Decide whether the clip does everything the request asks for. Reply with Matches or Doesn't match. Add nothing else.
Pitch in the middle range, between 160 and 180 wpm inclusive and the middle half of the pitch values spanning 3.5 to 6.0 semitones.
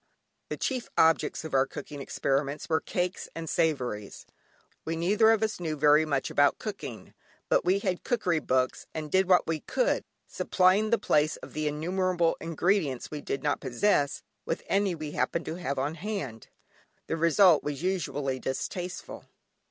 Matches